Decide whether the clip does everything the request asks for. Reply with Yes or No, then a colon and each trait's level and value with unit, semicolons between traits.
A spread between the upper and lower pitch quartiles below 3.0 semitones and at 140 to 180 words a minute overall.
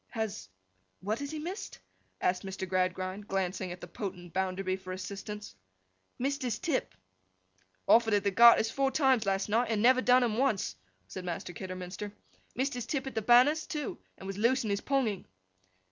No: average, 5.2 semitones; average, 175 wpm